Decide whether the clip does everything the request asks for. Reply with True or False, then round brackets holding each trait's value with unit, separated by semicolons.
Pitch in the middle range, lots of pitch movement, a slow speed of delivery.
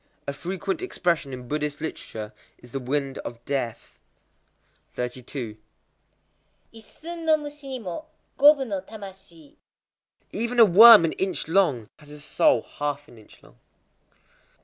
True (165 Hz; 8.7 semitones; 130 wpm)